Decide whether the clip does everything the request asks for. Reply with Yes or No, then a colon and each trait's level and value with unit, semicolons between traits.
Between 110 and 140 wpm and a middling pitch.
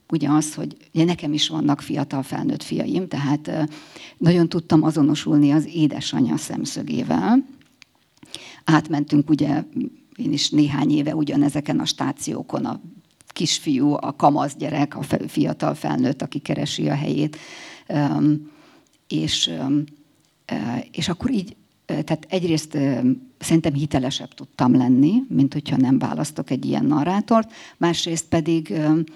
Yes: average, 115 wpm; medium, 155 Hz